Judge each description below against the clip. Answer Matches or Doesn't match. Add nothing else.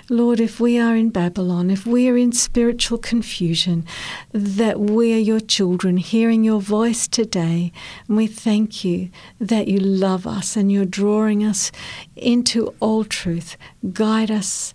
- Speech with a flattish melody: Doesn't match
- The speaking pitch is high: Matches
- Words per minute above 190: Doesn't match